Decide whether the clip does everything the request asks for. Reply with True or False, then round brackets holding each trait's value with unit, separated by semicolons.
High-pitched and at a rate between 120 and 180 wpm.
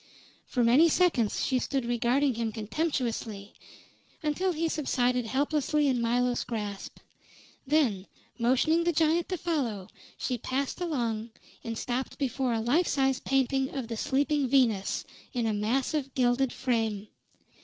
True (255 Hz; 135 wpm)